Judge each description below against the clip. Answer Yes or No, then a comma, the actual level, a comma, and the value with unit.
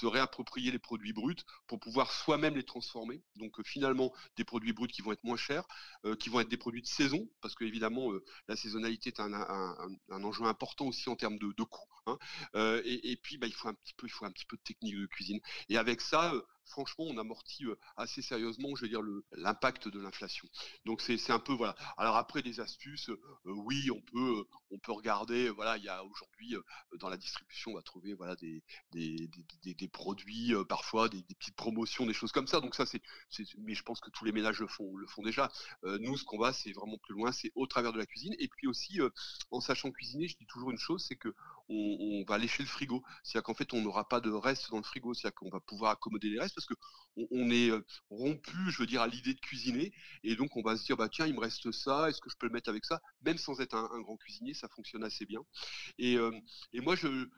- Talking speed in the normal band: No, fast, 255 wpm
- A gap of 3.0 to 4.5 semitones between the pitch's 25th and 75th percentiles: Yes, average, 3.3 semitones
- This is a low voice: Yes, low, 115 Hz